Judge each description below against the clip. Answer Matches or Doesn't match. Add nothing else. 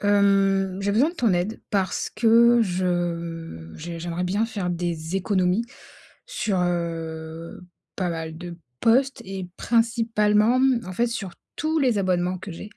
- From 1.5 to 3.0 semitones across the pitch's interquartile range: Doesn't match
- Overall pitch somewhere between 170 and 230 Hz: Matches